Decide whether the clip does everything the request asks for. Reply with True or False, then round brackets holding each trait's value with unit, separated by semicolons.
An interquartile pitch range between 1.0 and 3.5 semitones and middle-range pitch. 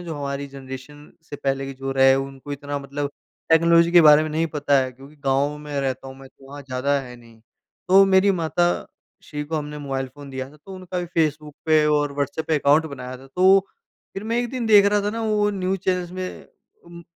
False (4.3 semitones; 150 Hz)